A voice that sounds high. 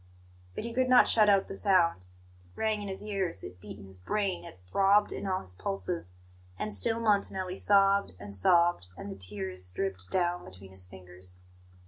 No: medium, 170 Hz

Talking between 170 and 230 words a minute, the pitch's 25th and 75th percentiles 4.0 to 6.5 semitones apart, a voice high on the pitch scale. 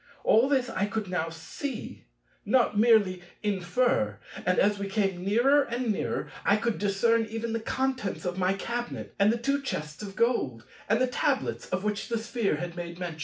Yes: average, 185 wpm; average, 4.4 semitones; high, 210 Hz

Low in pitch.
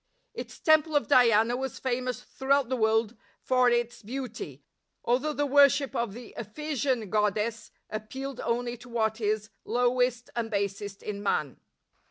No: high, 240 Hz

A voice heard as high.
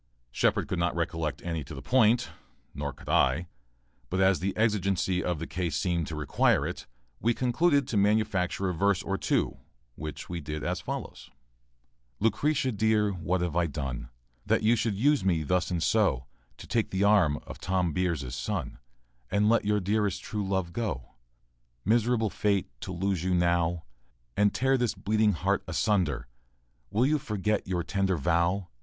No: very low, 95 Hz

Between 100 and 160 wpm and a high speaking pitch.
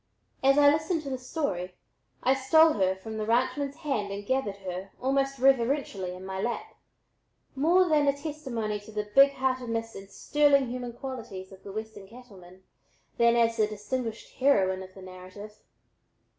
No: average, 170 wpm; high, 235 Hz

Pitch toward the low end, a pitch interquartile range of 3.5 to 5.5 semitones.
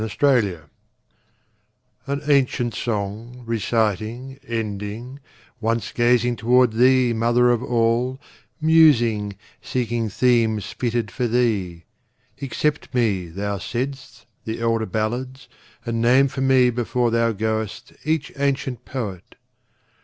No: low, 120 Hz; narrow, 2.6 semitones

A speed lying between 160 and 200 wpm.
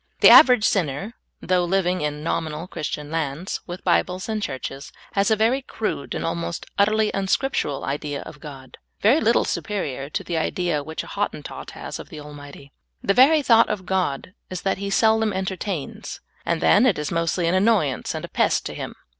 Yes: average, 190 wpm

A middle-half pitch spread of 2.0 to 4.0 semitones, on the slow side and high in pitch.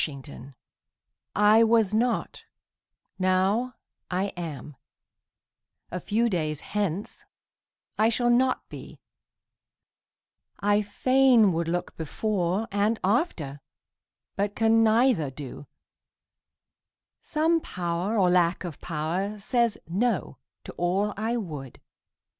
No: average, 4.8 semitones; slow, 105 wpm; high, 200 Hz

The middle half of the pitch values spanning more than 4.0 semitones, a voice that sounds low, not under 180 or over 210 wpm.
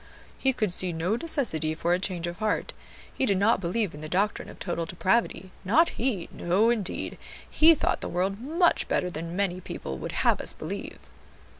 No: average, 5.0 semitones; high, 190 Hz; average, 190 wpm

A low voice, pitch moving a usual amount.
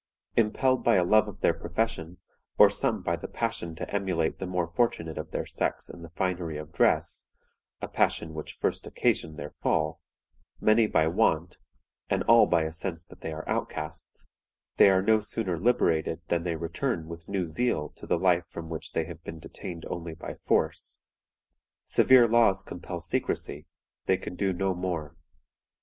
Yes: very low, 85 Hz; average, 3.3 semitones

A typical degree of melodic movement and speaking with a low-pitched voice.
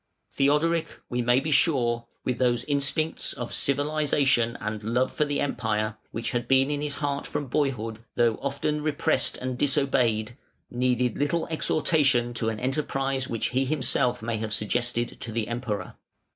Yes: average, 3.4 semitones; low, 125 Hz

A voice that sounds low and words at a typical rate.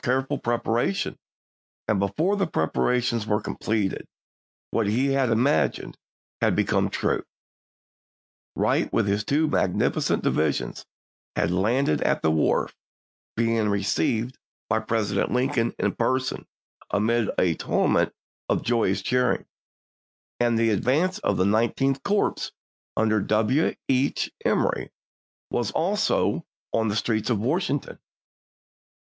No: low, 115 Hz; slow, 125 wpm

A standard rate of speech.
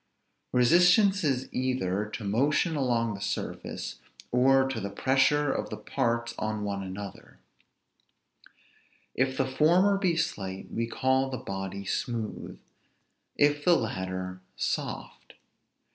No: slow, 120 wpm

